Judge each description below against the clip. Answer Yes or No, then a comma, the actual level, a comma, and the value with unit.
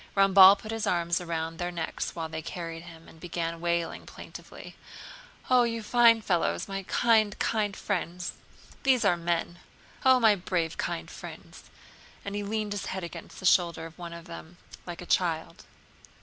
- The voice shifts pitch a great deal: No, average, 3.5 semitones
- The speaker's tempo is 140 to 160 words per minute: No, average, 175 wpm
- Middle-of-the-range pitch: Yes, medium, 175 Hz